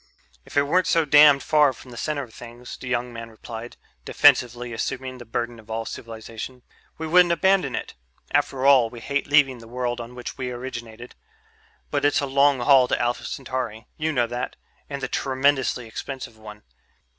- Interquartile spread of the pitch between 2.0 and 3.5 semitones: Yes, average, 3.1 semitones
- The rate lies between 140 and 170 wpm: No, average, 185 wpm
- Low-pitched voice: Yes, low, 125 Hz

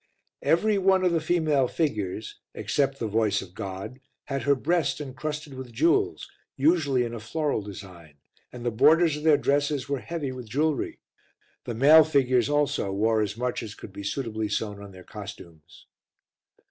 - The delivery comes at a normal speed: Yes, average, 170 wpm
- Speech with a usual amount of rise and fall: No, wide, 6.0 semitones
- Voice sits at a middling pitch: No, low, 130 Hz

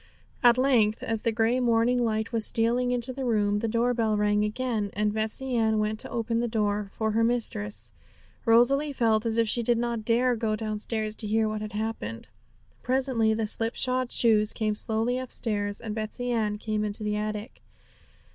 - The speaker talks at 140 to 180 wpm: No, average, 190 wpm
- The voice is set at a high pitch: Yes, high, 225 Hz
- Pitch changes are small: Yes, narrow, 2.1 semitones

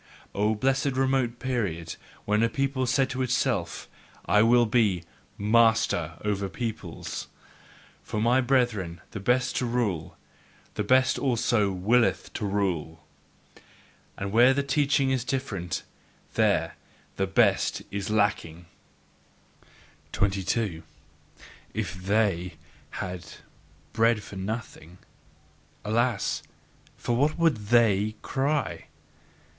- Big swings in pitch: No, average, 4.5 semitones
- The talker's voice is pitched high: No, low, 110 Hz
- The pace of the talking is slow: Yes, slow, 105 wpm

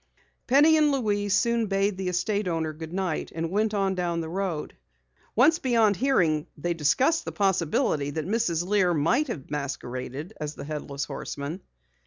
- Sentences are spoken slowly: No, average, 160 wpm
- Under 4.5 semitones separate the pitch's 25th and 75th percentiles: No, wide, 5.4 semitones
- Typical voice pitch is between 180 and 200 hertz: Yes, medium, 185 Hz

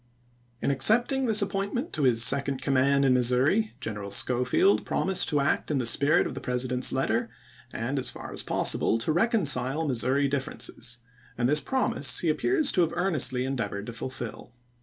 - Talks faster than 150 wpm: Yes, average, 175 wpm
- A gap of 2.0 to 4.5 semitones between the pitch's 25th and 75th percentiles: No, wide, 5.6 semitones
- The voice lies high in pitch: No, low, 135 Hz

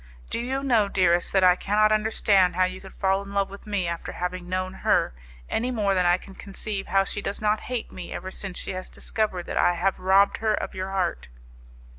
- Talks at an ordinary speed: No, fast, 225 wpm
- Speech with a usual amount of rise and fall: No, narrow, 2.3 semitones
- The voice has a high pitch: Yes, high, 195 Hz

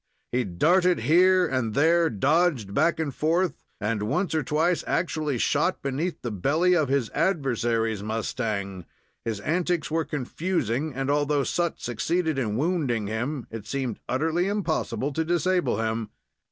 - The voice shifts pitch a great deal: Yes, wide, 6.6 semitones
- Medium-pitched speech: Yes, medium, 145 Hz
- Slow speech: No, average, 145 wpm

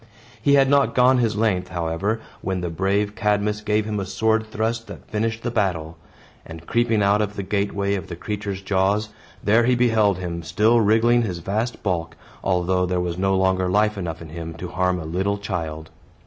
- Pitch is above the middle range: No, low, 100 Hz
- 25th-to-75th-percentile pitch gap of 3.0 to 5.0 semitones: Yes, average, 3.3 semitones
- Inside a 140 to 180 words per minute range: No, average, 195 wpm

